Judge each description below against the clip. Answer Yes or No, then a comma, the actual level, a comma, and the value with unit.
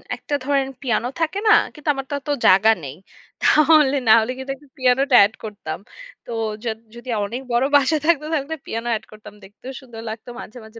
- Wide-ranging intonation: No, average, 4.5 semitones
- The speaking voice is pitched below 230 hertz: No, very high, 255 Hz